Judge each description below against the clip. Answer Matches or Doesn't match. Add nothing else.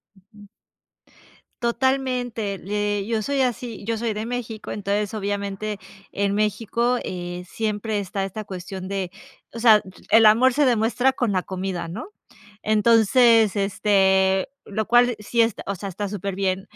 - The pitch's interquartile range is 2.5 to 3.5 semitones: Matches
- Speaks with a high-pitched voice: Matches